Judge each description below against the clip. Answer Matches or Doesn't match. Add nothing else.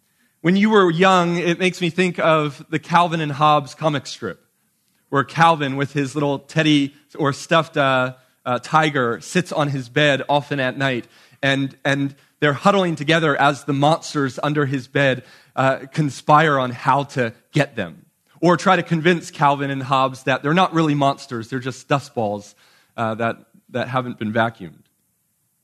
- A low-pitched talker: Doesn't match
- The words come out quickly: Doesn't match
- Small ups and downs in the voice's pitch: Doesn't match